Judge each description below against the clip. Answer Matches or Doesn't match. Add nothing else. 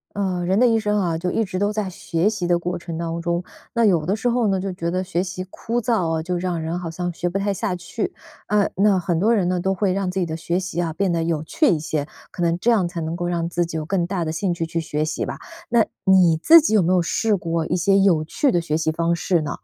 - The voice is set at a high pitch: Doesn't match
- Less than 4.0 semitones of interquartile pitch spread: Matches